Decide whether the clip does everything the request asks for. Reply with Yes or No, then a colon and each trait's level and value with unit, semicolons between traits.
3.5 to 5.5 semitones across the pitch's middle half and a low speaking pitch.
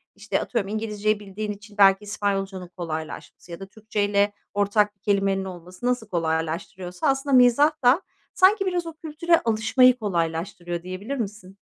No: average, 4.4 semitones; high, 205 Hz